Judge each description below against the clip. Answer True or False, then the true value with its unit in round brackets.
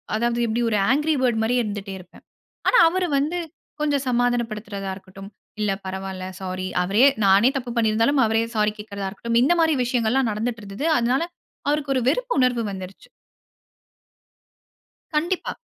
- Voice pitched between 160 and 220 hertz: False (230 Hz)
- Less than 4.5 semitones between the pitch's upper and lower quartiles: False (4.8 semitones)